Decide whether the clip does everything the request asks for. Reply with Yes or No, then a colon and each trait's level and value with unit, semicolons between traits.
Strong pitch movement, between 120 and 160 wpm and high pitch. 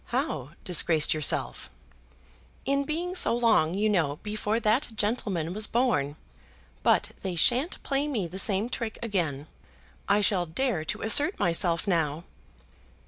Yes: wide, 6.4 semitones; average, 140 wpm; high, 205 Hz